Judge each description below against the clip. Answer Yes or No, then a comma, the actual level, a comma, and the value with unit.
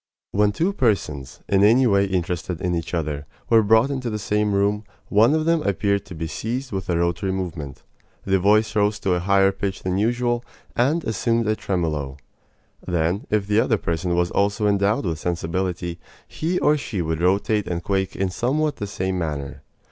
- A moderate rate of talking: Yes, average, 185 wpm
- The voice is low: Yes, low, 100 Hz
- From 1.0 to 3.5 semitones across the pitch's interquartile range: No, average, 4.0 semitones